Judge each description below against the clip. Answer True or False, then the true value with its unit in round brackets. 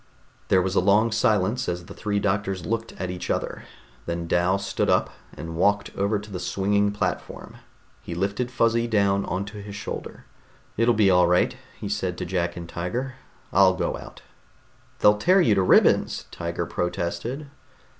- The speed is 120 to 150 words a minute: False (170 wpm)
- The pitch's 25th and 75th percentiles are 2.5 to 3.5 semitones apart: True (2.9 semitones)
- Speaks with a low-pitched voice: True (100 Hz)